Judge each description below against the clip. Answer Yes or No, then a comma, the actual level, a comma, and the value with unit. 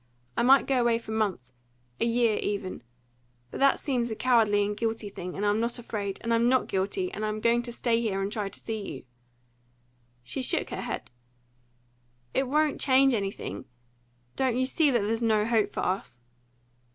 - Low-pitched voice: No, high, 225 Hz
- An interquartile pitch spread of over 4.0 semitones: No, average, 3.1 semitones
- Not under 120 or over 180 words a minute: No, average, 190 wpm